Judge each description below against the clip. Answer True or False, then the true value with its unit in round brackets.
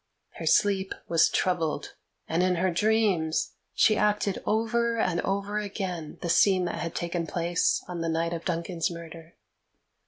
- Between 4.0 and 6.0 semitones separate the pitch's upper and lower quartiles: False (3.3 semitones)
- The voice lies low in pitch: False (180 Hz)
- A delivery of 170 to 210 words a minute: False (155 wpm)